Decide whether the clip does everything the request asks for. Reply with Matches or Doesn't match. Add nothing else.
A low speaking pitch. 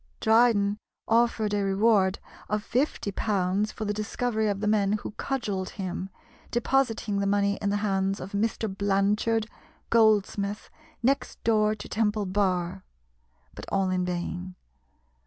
Doesn't match